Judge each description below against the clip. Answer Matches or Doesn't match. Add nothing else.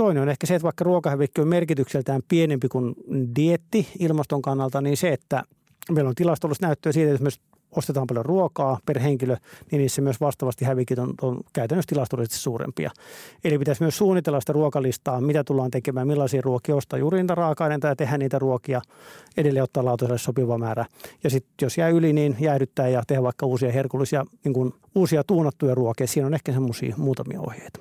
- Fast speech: Matches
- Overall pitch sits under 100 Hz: Doesn't match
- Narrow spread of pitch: Doesn't match